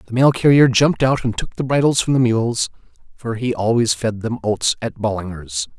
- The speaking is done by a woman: No, male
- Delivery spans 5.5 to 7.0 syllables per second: No, 5.2 syllables/s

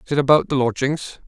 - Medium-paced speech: No, fast, 235 wpm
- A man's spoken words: Yes, male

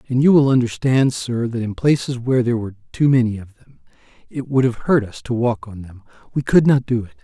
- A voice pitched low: Yes, low, 125 Hz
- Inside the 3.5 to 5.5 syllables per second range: No, 6.0 syllables/s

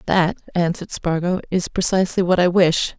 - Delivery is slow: No, average, 160 wpm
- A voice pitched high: No, medium, 180 Hz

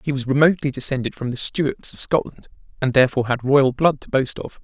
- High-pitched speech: No, low, 135 Hz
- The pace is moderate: No, fast, 220 wpm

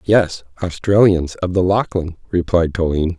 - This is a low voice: Yes, very low, 90 Hz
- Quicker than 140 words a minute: No, slow, 130 wpm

